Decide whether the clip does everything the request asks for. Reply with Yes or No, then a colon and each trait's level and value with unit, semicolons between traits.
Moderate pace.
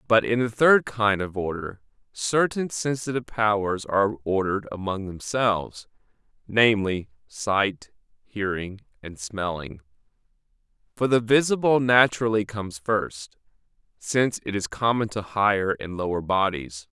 No: slow, 120 wpm